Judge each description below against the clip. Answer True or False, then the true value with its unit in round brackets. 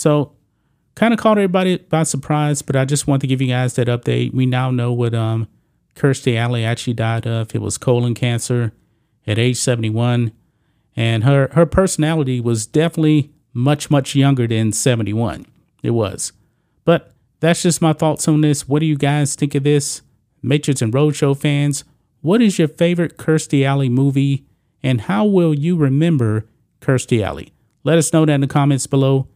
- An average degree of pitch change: True (3.9 semitones)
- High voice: False (140 Hz)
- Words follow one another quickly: False (180 wpm)